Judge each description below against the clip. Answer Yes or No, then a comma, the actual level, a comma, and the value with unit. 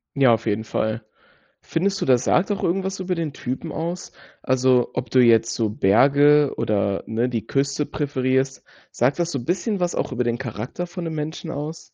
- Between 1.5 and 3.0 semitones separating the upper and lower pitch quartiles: No, wide, 5.6 semitones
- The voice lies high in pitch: No, low, 135 Hz